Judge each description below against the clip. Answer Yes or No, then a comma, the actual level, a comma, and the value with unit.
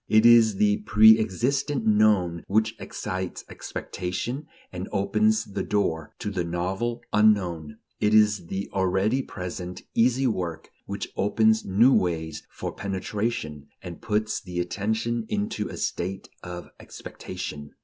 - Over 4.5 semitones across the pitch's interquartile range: No, average, 3.5 semitones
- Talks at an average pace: No, slow, 130 wpm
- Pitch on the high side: No, low, 105 Hz